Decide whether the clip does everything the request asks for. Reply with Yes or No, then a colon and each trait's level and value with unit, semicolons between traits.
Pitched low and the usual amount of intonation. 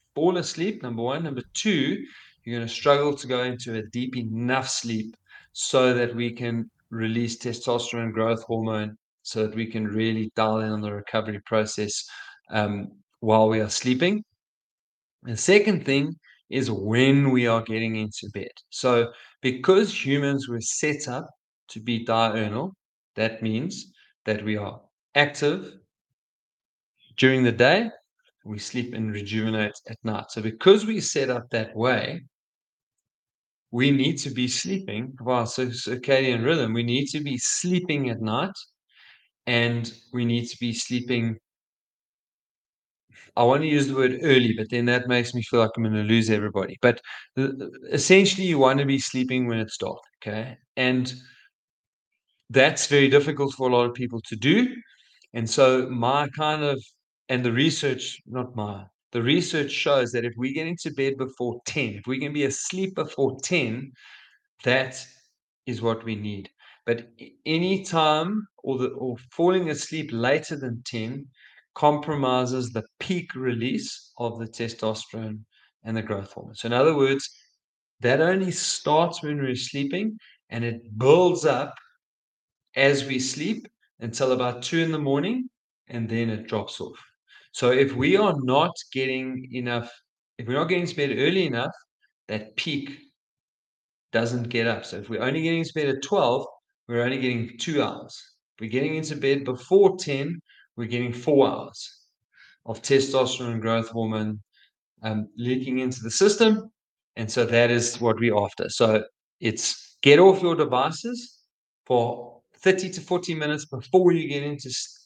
Yes: low, 125 Hz; average, 4.0 semitones